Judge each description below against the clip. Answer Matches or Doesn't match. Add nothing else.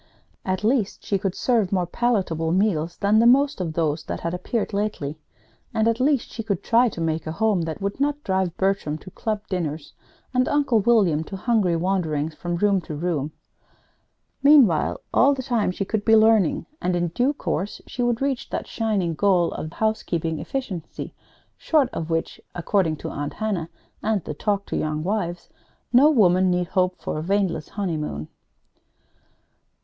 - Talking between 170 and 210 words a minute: Matches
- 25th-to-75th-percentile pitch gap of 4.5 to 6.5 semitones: Matches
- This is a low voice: Doesn't match